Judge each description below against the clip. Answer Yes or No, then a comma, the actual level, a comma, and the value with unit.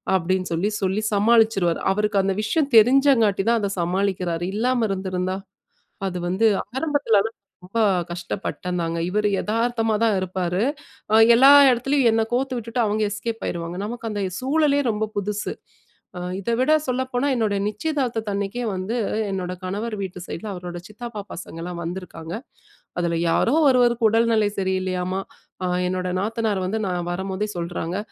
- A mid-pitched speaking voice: No, high, 210 Hz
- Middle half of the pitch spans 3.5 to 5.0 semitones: Yes, average, 4.0 semitones